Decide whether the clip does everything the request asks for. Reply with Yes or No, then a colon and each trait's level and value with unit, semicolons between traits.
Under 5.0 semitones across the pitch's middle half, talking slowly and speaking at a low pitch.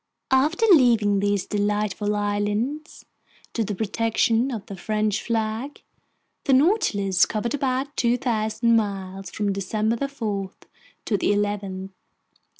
No: average, 2.9 semitones; slow, 115 wpm; high, 215 Hz